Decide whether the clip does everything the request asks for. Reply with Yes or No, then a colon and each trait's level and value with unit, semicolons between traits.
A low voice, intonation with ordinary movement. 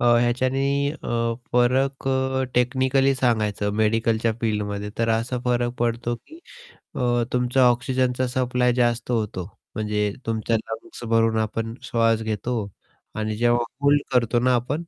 No: low, 120 Hz; narrow, 2.0 semitones